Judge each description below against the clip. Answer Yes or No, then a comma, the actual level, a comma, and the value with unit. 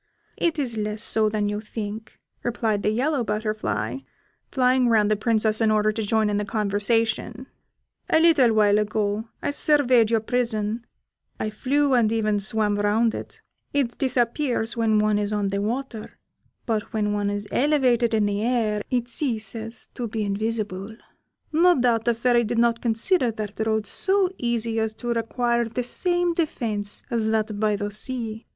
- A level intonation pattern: Yes, narrow, 2.3 semitones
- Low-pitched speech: No, high, 225 Hz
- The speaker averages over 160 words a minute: Yes, average, 170 wpm